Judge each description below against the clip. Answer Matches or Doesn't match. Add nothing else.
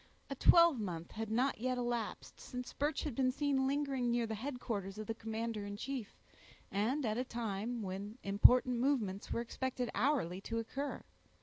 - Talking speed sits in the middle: Matches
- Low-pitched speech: Doesn't match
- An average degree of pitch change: Matches